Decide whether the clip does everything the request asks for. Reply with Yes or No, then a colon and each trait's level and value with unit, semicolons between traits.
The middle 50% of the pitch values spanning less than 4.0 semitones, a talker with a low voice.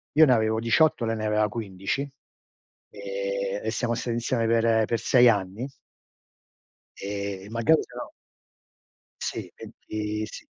Yes: narrow, 2.5 semitones; low, 110 Hz